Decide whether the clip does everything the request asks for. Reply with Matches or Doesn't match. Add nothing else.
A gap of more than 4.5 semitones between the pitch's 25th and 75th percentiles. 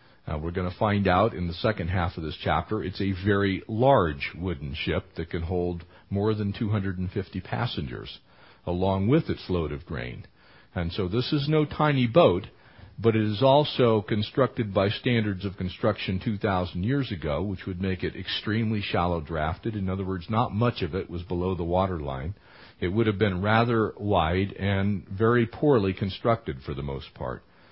Doesn't match